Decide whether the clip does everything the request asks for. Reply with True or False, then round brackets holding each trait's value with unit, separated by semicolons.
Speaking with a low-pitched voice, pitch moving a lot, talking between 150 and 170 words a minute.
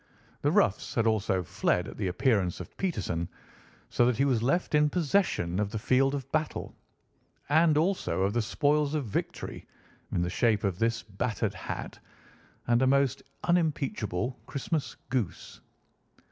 True (125 Hz; 6.2 semitones; 155 wpm)